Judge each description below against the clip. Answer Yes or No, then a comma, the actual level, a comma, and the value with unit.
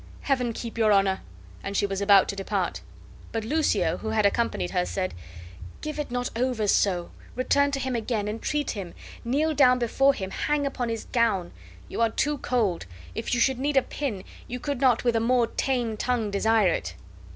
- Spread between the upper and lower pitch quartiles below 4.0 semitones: No, average, 4.4 semitones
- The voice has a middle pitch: No, high, 235 Hz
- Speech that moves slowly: No, average, 195 wpm